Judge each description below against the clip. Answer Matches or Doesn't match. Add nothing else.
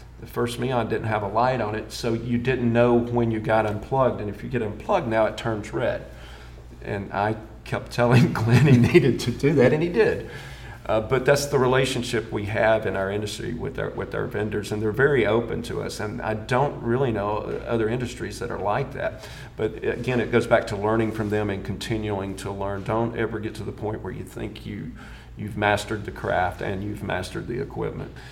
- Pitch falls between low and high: Doesn't match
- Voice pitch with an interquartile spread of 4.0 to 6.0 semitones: Doesn't match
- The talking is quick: Matches